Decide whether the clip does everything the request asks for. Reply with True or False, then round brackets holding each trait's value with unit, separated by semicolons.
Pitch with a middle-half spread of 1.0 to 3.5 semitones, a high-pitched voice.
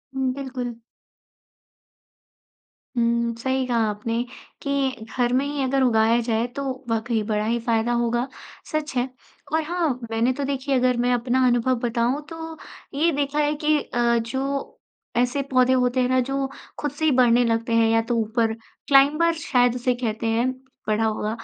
True (2.8 semitones; 245 Hz)